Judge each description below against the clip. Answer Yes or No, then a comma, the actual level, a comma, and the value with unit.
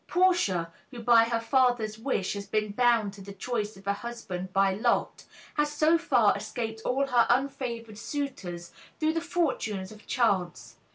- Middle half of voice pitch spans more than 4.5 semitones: Yes, average, 5.0 semitones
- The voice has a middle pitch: No, high, 230 Hz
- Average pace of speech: Yes, average, 165 wpm